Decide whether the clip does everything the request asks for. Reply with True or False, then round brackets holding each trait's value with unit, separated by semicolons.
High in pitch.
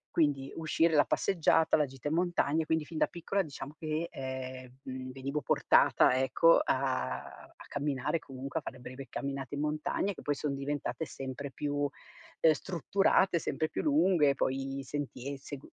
False (145 Hz)